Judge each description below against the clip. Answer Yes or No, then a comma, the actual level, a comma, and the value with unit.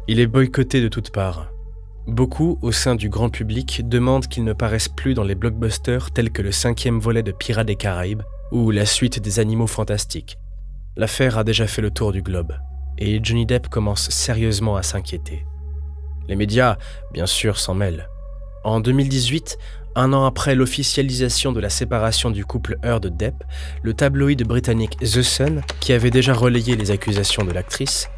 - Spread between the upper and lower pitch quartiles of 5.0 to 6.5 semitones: No, average, 4.4 semitones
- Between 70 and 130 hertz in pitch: Yes, low, 110 Hz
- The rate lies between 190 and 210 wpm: No, average, 170 wpm